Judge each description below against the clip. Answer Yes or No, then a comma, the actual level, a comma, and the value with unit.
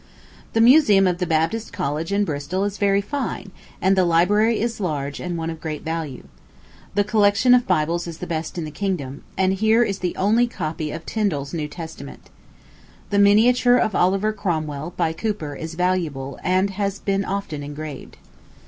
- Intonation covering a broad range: No, average, 4.4 semitones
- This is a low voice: No, medium, 185 Hz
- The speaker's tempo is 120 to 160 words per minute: No, average, 175 wpm